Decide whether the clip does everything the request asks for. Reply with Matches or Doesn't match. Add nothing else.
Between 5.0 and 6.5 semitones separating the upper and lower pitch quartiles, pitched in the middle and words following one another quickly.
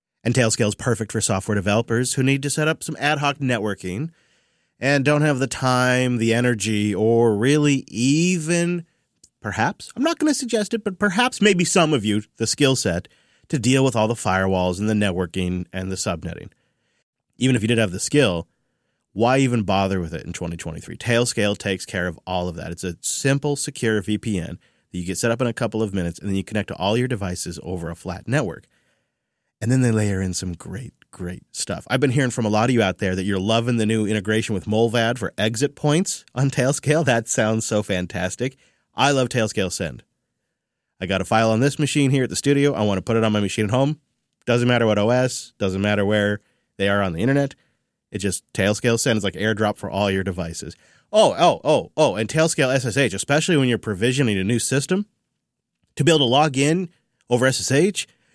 Doesn't match